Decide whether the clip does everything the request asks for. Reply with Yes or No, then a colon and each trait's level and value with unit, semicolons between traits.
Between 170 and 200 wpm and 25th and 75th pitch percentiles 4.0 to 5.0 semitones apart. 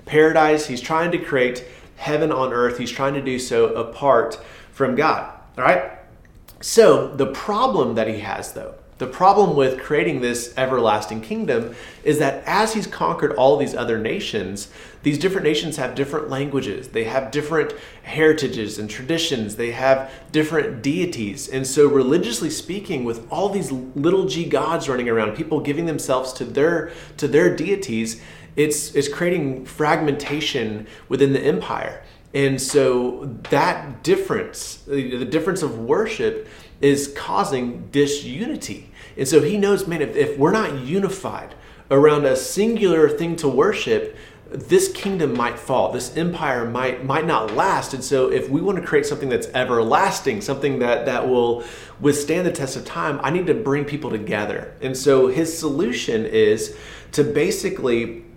No: average, 155 wpm; average, 4.3 semitones